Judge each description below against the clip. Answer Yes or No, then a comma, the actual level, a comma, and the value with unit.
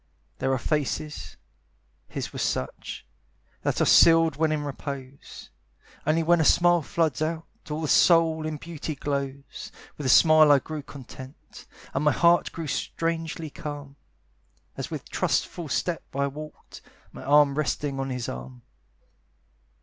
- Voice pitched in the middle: Yes, medium, 150 Hz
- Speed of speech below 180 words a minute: Yes, average, 145 wpm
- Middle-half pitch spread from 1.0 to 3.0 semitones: Yes, narrow, 2.6 semitones